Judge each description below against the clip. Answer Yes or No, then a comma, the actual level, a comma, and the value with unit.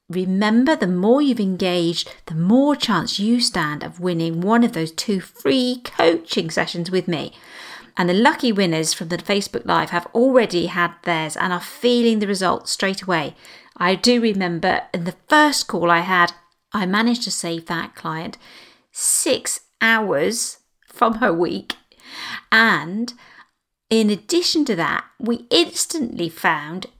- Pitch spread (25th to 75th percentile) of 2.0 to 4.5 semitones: No, wide, 5.4 semitones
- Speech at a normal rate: Yes, average, 150 wpm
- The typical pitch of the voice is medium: No, high, 195 Hz